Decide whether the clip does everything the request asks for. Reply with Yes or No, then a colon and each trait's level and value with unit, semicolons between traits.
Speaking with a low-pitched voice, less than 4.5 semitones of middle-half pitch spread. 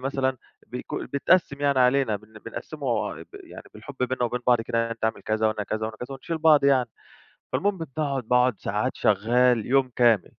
Yes: low, 125 Hz; average, 3.5 semitones